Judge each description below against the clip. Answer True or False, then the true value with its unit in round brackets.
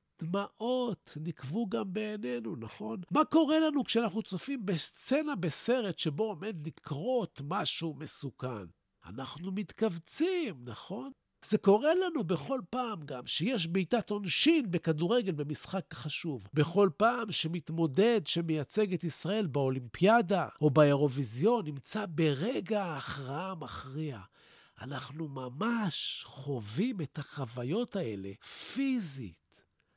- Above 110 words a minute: False (105 wpm)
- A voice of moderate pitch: True (175 Hz)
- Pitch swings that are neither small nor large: False (7.5 semitones)